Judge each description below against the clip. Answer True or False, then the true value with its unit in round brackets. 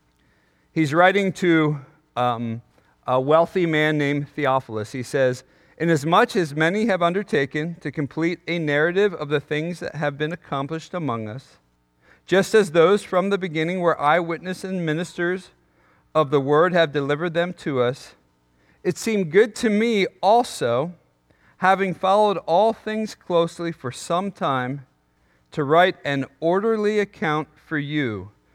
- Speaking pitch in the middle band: True (160 Hz)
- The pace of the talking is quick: False (145 wpm)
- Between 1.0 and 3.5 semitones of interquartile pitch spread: False (4.8 semitones)